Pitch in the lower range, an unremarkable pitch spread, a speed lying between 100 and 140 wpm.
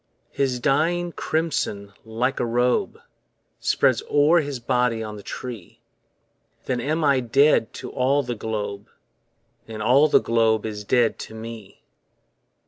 Yes: low, 120 Hz; average, 4.0 semitones; slow, 135 wpm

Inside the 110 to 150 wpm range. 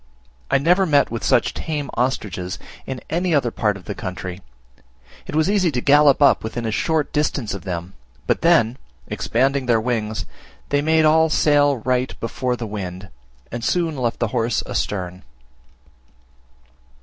No: average, 160 wpm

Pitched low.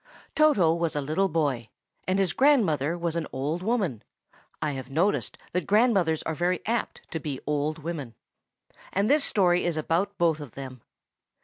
No: medium, 165 Hz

